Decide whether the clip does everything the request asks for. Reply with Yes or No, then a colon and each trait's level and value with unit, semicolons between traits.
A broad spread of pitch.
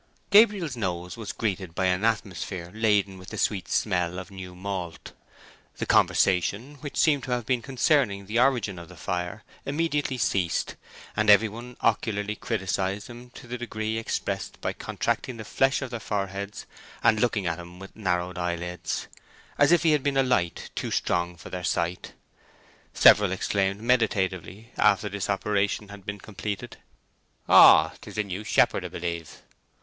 No: average, 4.2 semitones